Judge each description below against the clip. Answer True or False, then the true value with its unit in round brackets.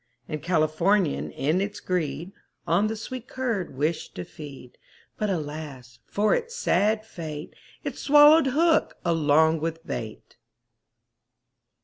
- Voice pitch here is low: False (170 Hz)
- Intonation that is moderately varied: False (5.9 semitones)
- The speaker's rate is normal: False (120 wpm)